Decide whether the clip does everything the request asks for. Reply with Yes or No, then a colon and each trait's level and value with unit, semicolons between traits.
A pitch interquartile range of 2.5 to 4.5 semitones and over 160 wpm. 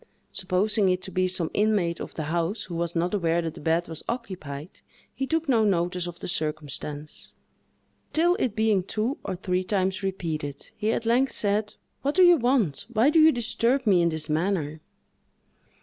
No: average, 4.9 semitones; average, 185 wpm